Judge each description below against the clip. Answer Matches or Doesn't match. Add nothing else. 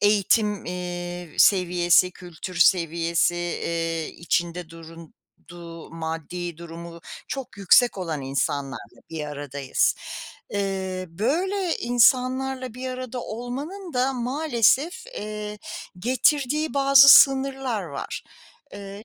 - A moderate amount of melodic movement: Doesn't match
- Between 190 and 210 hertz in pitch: Matches